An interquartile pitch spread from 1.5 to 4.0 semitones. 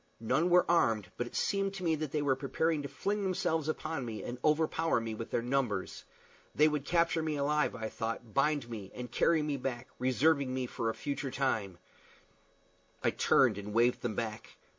No: average, 5.1 semitones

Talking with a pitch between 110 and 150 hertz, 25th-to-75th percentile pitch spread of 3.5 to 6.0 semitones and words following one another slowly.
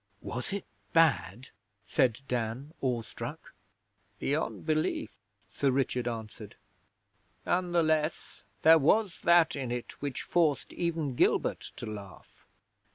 Yes: medium, 140 Hz; average, 5.1 semitones; slow, 115 wpm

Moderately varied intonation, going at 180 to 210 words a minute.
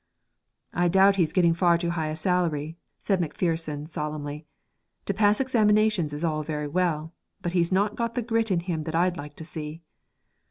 Yes: average, 3.8 semitones; average, 185 wpm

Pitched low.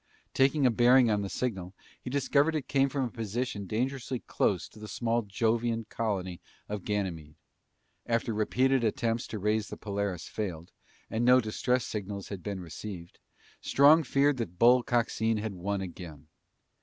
Yes: low, 110 Hz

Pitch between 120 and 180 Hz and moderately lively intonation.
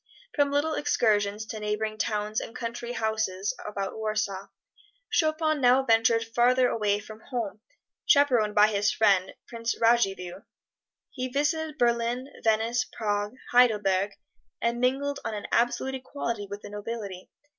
No: high, 225 Hz; average, 3.2 semitones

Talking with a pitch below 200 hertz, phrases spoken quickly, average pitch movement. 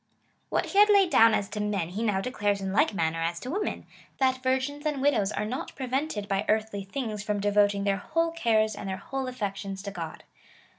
No: high, 215 Hz; fast, 215 wpm; average, 4.9 semitones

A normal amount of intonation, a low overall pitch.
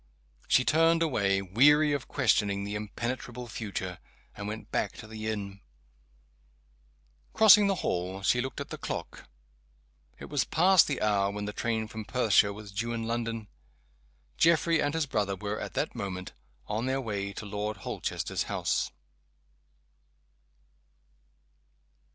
Yes: average, 4.6 semitones; low, 110 Hz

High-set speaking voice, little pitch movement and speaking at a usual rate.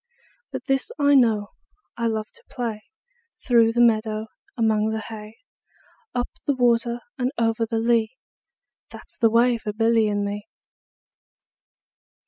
Yes: high, 225 Hz; narrow, 1.7 semitones; average, 145 wpm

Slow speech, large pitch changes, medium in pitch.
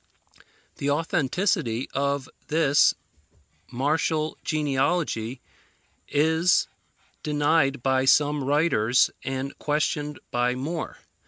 No: slow, 80 wpm; average, 2.7 semitones; medium, 145 Hz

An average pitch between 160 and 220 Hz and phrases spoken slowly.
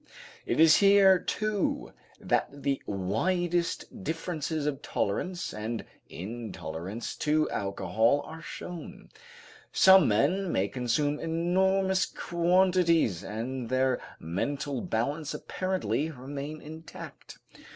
No: medium, 150 Hz; slow, 100 wpm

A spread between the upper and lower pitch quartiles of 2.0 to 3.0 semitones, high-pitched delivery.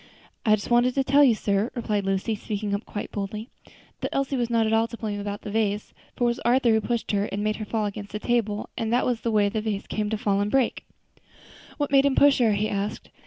Yes: narrow, 2.6 semitones; high, 220 Hz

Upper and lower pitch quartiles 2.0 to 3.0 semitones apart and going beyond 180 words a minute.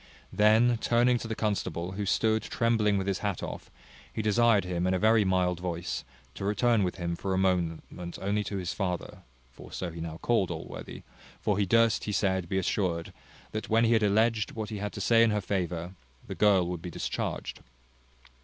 No: average, 3.4 semitones; average, 200 wpm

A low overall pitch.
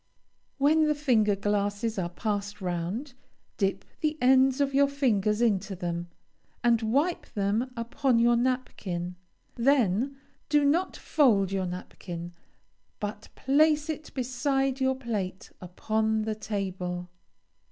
No: high, 225 Hz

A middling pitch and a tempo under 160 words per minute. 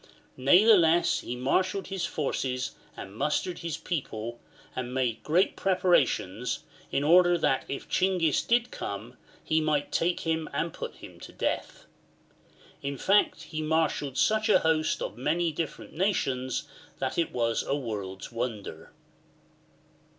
Yes: medium, 155 Hz; average, 140 wpm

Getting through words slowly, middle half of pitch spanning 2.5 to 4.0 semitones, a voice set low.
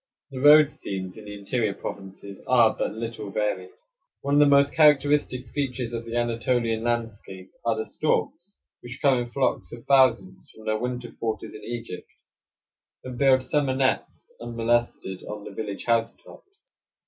No: average, 160 wpm; average, 3.3 semitones; low, 120 Hz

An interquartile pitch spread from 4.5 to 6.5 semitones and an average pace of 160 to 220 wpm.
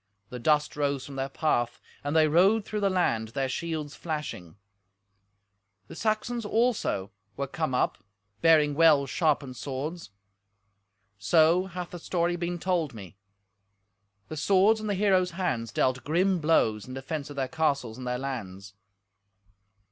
No: average, 5.2 semitones; average, 150 wpm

